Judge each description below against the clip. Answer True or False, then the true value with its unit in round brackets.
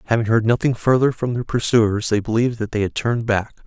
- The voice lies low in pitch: True (115 Hz)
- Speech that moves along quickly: True (230 wpm)